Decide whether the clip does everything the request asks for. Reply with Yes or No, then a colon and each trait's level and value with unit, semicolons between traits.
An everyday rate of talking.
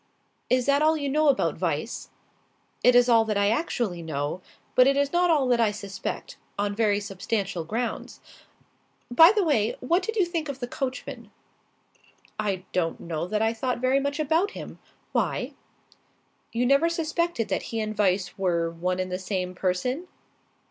Yes: average, 175 wpm